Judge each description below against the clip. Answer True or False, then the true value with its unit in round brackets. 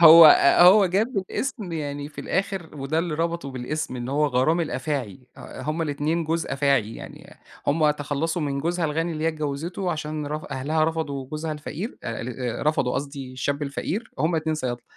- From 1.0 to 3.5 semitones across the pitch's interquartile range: True (2.9 semitones)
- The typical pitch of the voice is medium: True (155 Hz)